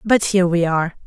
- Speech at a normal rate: No, fast, 225 wpm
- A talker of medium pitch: Yes, medium, 180 Hz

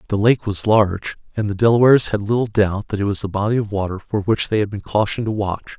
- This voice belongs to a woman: No, male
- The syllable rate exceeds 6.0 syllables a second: Yes, 6.3 syllables/s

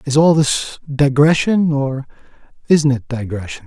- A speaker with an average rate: No, slow, 130 wpm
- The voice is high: No, medium, 140 Hz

